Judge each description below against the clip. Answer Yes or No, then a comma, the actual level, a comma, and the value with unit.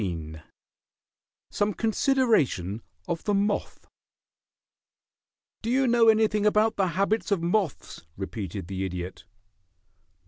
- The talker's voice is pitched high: Yes, high, 200 Hz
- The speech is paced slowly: Yes, slow, 105 wpm